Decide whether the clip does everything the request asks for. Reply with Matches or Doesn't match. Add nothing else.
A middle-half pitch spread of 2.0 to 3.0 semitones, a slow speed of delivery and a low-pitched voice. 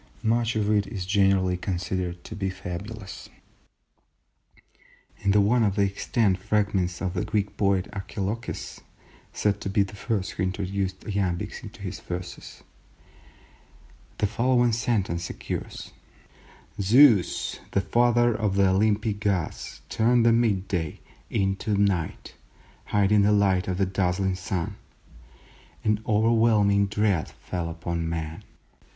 Matches